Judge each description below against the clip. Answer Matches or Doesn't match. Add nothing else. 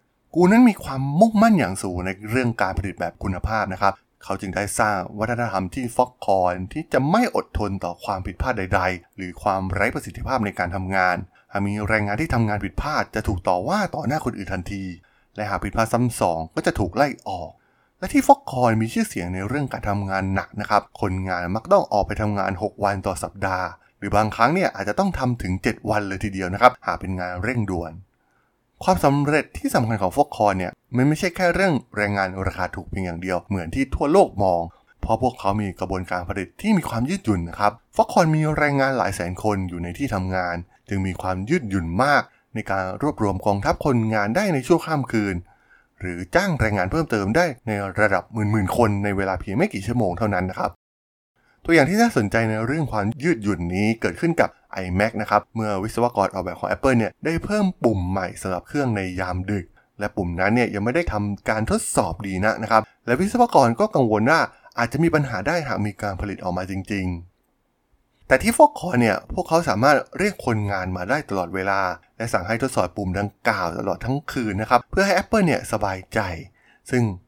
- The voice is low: Matches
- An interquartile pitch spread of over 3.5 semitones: Matches